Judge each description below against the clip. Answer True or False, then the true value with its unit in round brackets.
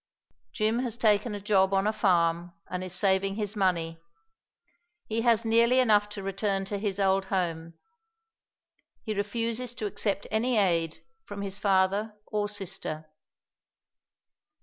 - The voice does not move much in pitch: True (2.3 semitones)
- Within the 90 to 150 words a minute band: True (140 wpm)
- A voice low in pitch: False (200 Hz)